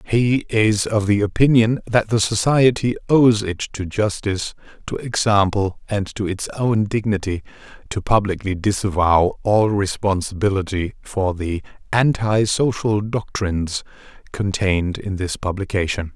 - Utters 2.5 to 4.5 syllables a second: Yes, 4.4 syllables/s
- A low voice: Yes, low, 100 Hz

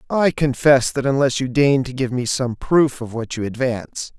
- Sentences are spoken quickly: Yes, fast, 215 wpm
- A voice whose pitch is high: No, low, 130 Hz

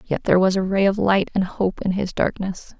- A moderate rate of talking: No, fast, 260 wpm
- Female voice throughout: Yes, female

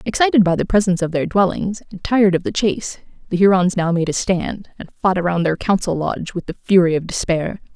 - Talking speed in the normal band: No, fast, 225 wpm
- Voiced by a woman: Yes, female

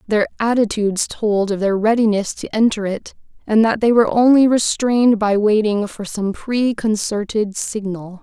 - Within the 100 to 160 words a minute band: Yes, average, 155 wpm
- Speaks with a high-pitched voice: Yes, high, 215 Hz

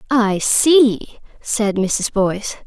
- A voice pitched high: Yes, high, 220 Hz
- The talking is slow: Yes, slow, 110 wpm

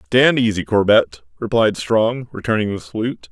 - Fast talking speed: No, average, 145 wpm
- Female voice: No, male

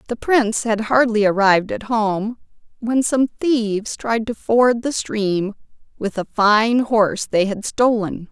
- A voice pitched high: Yes, high, 220 Hz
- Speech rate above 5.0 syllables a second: No, 4.0 syllables/s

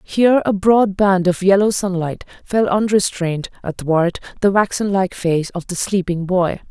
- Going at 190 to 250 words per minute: No, average, 160 wpm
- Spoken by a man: No, female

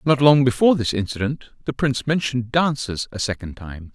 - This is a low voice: Yes, low, 125 Hz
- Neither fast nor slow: Yes, average, 180 wpm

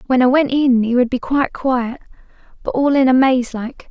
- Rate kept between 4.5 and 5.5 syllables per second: Yes, 5.1 syllables/s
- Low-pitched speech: No, very high, 255 Hz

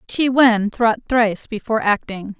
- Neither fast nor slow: Yes, average, 150 wpm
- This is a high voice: Yes, high, 225 Hz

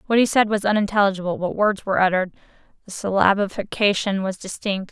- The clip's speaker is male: No, female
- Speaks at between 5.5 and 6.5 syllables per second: Yes, 6.3 syllables/s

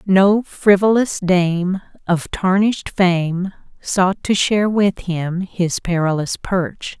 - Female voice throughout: Yes, female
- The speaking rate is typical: No, slow, 120 wpm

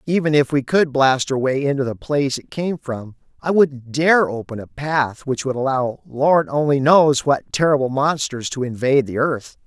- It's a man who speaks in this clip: Yes, male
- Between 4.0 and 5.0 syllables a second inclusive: Yes, 4.7 syllables/s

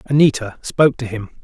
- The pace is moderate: Yes, average, 170 wpm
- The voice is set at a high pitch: No, low, 125 Hz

